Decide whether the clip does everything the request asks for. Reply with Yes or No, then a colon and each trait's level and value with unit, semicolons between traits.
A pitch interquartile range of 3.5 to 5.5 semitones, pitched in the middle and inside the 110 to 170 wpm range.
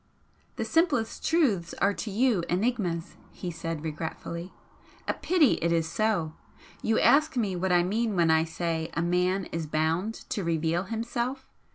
Yes: average, 5.2 semitones; medium, 180 Hz; average, 160 wpm